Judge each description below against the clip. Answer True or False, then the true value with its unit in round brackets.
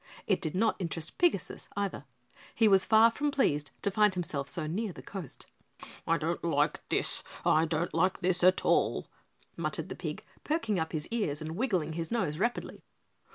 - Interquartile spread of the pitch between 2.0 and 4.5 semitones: False (5.2 semitones)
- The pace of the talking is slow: False (180 wpm)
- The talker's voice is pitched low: False (180 Hz)